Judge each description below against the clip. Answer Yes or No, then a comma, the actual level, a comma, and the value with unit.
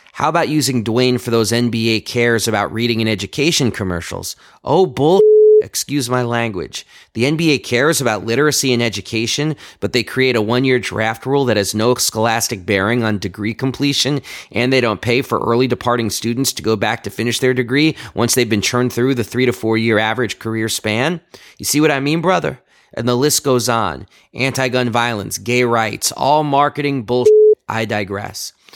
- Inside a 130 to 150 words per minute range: No, average, 185 wpm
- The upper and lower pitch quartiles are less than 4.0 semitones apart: Yes, average, 3.1 semitones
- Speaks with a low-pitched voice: Yes, low, 120 Hz